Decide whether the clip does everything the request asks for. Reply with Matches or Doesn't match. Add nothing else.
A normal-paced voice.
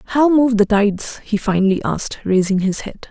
Matches